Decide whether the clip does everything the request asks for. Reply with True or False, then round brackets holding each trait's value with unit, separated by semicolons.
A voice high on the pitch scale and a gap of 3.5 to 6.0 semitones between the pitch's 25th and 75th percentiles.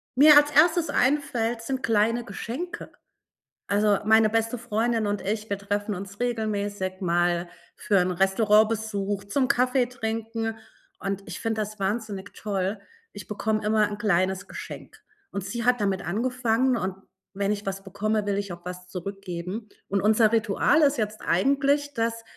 False (215 Hz; 2.7 semitones)